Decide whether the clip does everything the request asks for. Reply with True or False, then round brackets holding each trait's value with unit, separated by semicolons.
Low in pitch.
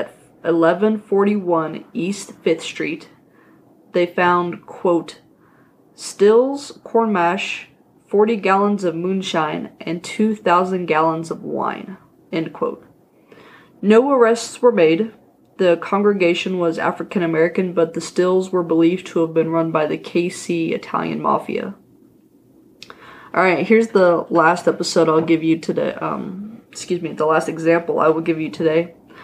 False (175 Hz)